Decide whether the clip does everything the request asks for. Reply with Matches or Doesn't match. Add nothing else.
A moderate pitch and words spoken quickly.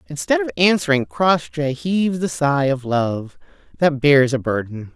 Doesn't match